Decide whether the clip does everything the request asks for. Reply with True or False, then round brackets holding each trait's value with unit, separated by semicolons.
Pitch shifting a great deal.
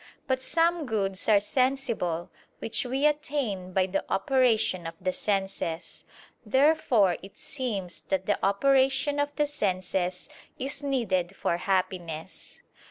True (6.4 semitones)